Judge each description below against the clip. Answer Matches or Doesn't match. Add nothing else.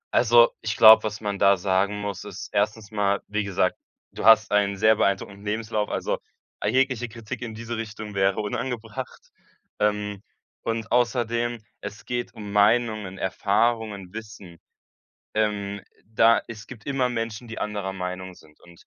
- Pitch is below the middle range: Matches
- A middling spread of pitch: Doesn't match